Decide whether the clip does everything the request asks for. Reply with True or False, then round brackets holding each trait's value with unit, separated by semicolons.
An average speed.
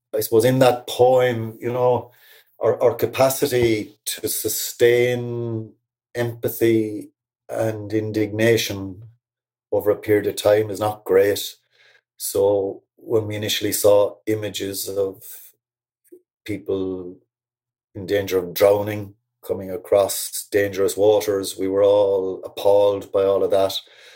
False (115 wpm)